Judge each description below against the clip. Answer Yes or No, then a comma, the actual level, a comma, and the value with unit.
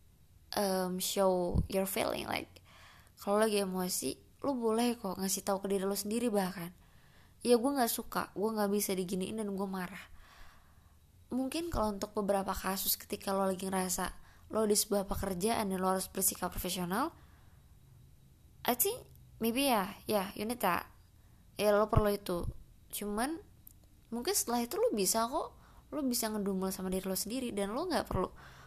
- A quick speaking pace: Yes, fast, 165 wpm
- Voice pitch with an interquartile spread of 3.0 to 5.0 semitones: Yes, average, 3.3 semitones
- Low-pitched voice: No, high, 200 Hz